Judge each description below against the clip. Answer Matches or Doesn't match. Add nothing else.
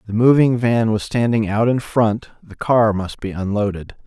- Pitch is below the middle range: Matches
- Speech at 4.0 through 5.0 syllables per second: Matches